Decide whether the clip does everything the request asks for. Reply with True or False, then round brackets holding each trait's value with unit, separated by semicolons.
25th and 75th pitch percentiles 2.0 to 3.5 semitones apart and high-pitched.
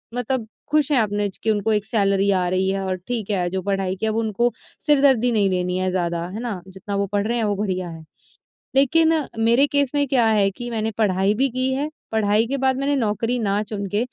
False (4.1 semitones; 215 Hz)